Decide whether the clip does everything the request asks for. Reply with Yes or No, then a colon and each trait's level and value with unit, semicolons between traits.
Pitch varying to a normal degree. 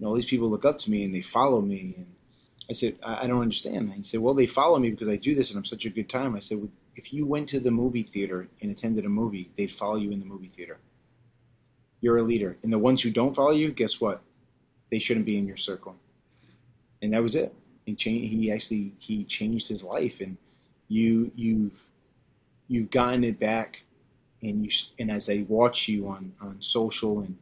Yes: average, 3.0 semitones